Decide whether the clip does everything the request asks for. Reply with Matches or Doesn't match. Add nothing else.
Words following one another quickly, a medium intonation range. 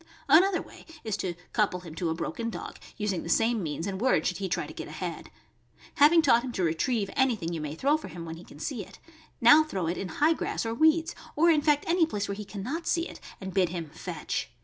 Doesn't match